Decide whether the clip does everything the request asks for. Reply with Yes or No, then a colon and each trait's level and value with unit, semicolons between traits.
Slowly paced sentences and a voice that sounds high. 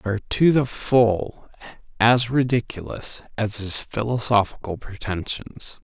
No: slow, 110 wpm; low, 110 Hz